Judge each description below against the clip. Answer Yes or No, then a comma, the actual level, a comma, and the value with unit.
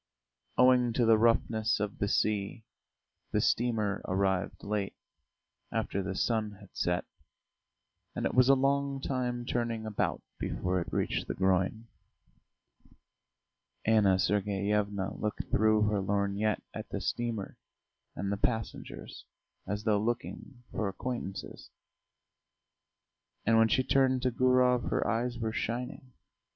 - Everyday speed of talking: No, slow, 125 wpm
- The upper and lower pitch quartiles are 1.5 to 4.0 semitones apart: Yes, average, 3.3 semitones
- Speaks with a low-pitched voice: Yes, low, 110 Hz